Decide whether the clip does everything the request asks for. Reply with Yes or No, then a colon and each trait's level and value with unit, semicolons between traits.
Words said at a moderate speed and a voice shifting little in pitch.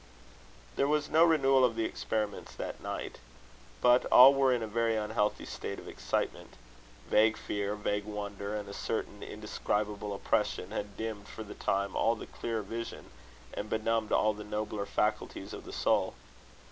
Yes: average, 165 wpm; narrow, 2.1 semitones